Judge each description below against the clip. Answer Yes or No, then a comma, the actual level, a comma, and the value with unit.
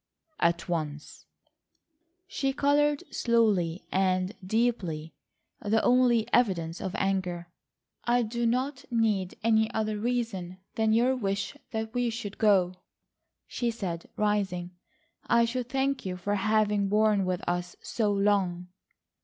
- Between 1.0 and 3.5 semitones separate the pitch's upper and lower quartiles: No, average, 4.3 semitones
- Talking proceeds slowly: Yes, slow, 120 wpm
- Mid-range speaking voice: No, high, 210 Hz